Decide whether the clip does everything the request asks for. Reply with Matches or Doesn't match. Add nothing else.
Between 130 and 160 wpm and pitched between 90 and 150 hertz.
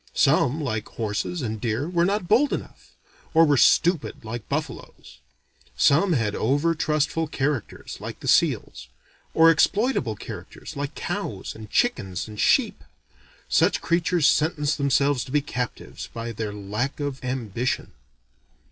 Matches